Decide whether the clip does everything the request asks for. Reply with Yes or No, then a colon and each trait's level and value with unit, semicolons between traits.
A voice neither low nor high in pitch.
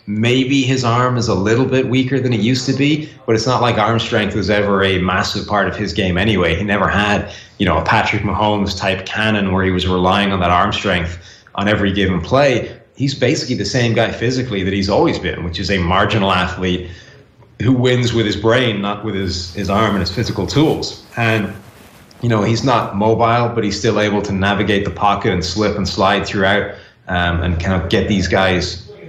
No: low, 105 Hz